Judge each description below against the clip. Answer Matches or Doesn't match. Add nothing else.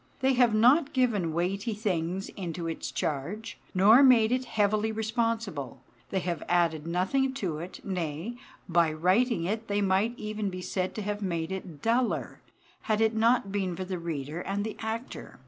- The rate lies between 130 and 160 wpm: Doesn't match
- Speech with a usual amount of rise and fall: Matches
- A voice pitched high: Matches